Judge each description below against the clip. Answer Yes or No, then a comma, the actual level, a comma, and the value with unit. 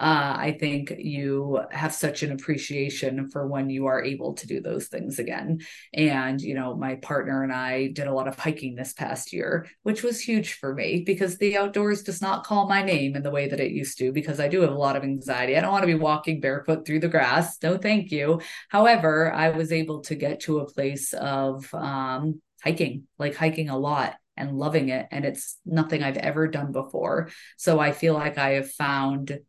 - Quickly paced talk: Yes, fast, 220 wpm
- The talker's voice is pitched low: No, medium, 145 Hz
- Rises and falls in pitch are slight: No, average, 3.0 semitones